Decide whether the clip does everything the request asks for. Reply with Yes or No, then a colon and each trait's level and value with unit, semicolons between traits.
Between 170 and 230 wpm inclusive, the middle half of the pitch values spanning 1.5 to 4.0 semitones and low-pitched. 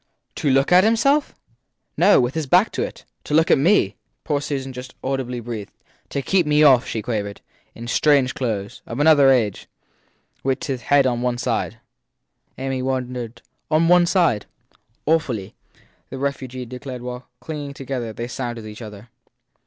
No: average, 160 wpm; average, 3.5 semitones; low, 130 Hz